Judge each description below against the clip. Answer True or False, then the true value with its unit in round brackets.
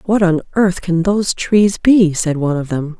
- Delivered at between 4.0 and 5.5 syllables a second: True (4.8 syllables/s)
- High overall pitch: False (180 Hz)